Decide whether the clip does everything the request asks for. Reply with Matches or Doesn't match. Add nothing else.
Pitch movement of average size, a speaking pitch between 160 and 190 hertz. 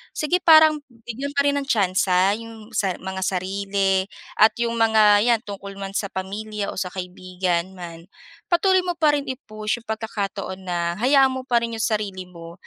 Doesn't match